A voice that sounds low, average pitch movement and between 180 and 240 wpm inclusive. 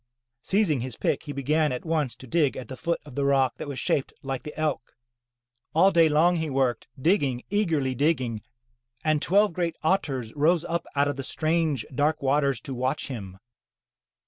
No: medium, 145 Hz; average, 3.7 semitones; average, 185 wpm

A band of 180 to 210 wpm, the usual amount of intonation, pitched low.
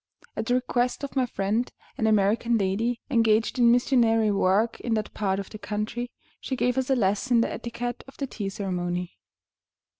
No: average, 185 wpm; average, 3.2 semitones; high, 225 Hz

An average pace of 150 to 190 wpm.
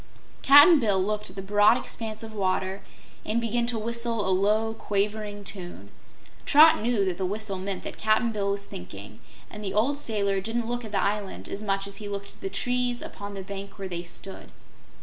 No: fast, 205 wpm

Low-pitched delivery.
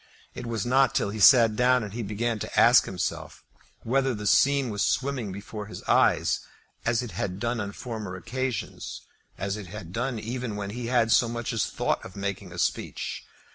Yes: low, 115 Hz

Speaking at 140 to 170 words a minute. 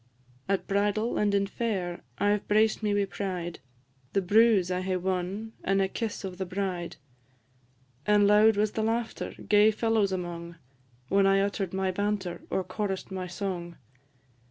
Yes: average, 160 wpm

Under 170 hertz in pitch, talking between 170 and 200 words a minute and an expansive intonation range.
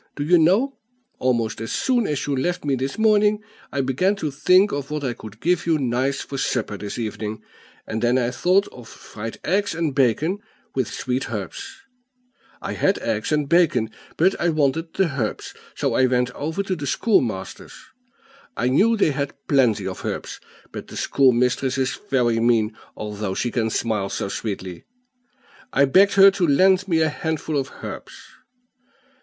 Yes: low, 135 Hz; average, 175 wpm; wide, 6.4 semitones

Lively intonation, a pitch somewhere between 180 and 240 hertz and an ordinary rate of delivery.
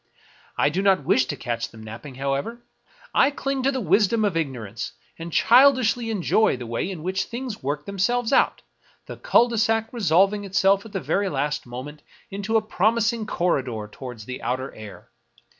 Yes: wide, 8.8 semitones; high, 190 Hz; average, 180 wpm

